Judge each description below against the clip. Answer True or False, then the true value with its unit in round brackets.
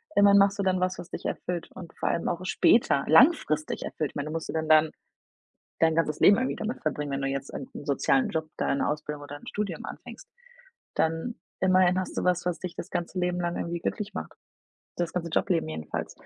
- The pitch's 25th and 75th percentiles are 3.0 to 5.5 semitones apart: True (3.3 semitones)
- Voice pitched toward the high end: False (170 Hz)